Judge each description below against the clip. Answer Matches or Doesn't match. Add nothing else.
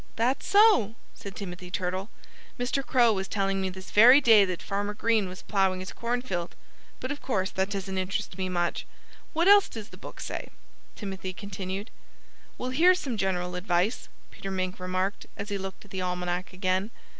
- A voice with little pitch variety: Doesn't match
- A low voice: Doesn't match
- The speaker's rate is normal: Matches